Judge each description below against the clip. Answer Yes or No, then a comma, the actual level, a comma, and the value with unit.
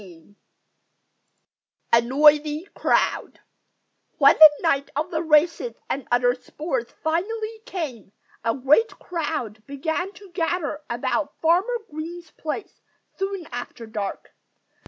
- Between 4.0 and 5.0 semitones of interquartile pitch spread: No, wide, 5.6 semitones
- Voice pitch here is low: No, very high, 305 Hz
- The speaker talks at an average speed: No, slow, 115 wpm